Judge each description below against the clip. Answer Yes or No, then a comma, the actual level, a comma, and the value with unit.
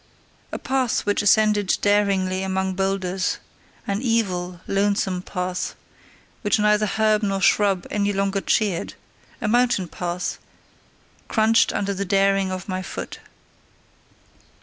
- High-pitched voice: Yes, high, 195 Hz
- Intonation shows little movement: Yes, narrow, 2.0 semitones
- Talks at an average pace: No, slow, 120 wpm